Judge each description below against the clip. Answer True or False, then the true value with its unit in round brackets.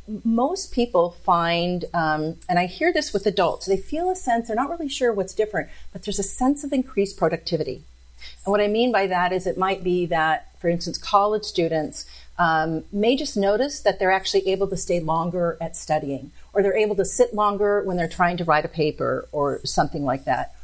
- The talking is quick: True (210 wpm)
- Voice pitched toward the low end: False (190 Hz)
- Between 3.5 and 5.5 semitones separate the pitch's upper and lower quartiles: True (4.1 semitones)